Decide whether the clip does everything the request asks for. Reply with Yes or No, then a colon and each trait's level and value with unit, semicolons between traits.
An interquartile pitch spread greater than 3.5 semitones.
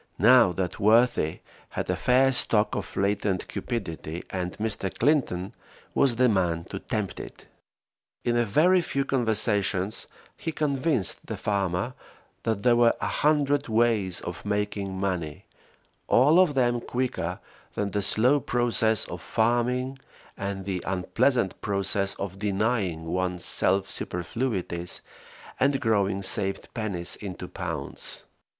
Yes: average, 4.6 semitones